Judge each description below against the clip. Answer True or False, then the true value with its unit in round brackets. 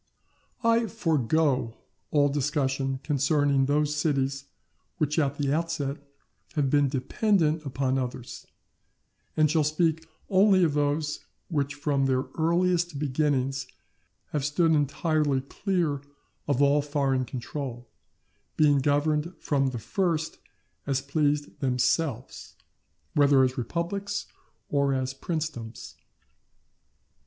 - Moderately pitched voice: True (145 Hz)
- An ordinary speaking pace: False (110 wpm)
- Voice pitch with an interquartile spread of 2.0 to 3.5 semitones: True (2.8 semitones)